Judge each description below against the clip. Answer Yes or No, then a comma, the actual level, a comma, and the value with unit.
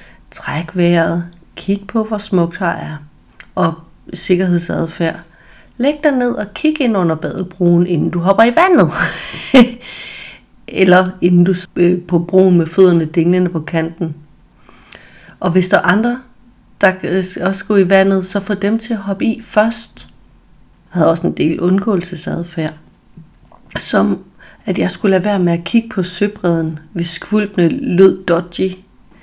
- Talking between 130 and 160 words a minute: Yes, average, 150 wpm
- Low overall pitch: No, medium, 185 Hz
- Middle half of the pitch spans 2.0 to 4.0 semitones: Yes, average, 3.4 semitones